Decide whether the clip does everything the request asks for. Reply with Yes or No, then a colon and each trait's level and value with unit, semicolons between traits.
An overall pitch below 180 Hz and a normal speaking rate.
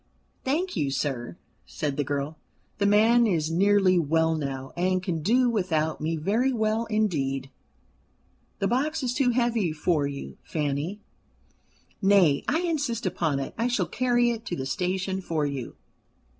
No: medium, 185 Hz; average, 155 wpm